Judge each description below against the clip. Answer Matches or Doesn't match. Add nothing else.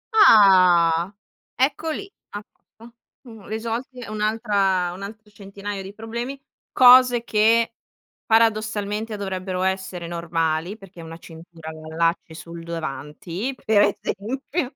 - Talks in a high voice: Matches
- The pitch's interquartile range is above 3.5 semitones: Matches